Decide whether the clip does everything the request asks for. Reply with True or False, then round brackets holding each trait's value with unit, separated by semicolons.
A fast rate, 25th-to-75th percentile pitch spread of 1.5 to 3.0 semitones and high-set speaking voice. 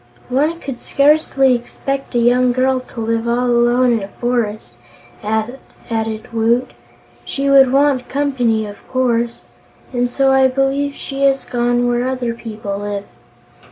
False (145 wpm; 2.6 semitones; 245 Hz)